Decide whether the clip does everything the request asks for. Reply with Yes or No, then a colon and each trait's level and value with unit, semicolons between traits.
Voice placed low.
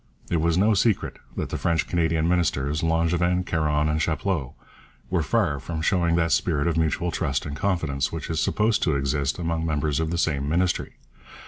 Yes: very low, 80 Hz